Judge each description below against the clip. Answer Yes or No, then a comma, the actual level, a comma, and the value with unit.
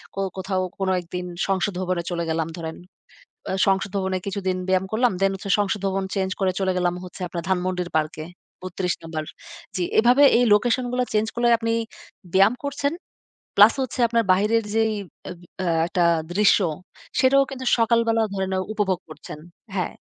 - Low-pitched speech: No, high, 195 Hz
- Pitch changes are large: No, average, 3.7 semitones